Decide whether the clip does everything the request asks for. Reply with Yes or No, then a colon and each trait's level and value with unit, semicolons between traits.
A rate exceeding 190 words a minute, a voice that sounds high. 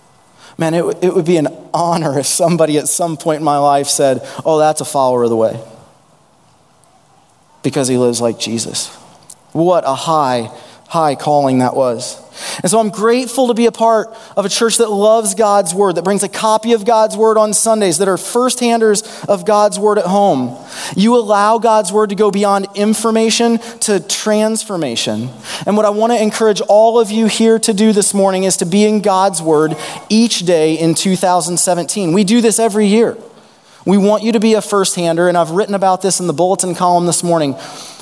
Yes: average, 200 wpm; high, 195 Hz